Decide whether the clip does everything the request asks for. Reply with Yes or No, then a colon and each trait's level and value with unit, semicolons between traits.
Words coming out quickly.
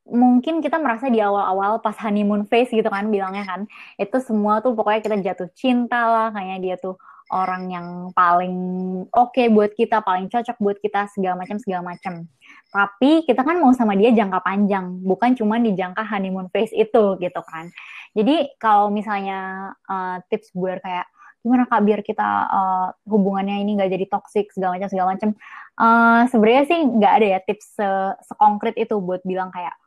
Yes: fast, 180 wpm